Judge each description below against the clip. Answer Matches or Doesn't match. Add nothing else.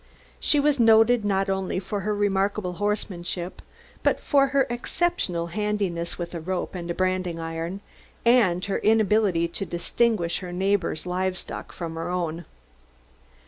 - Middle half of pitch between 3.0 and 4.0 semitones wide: Matches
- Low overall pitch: Doesn't match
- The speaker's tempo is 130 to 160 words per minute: Matches